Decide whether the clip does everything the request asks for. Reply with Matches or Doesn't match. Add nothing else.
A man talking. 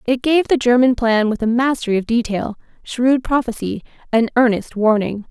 Doesn't match